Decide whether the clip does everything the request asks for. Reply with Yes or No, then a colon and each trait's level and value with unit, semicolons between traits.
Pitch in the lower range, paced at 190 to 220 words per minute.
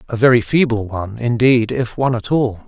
Yes: low, 120 Hz; average, 200 wpm